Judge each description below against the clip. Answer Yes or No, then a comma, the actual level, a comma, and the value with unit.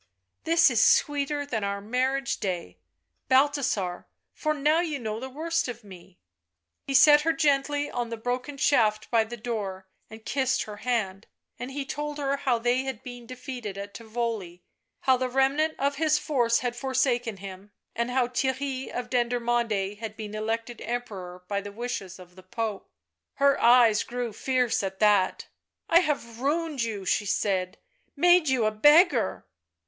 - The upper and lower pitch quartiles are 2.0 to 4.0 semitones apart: No, average, 4.5 semitones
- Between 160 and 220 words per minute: Yes, average, 170 wpm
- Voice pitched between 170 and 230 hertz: No, high, 240 Hz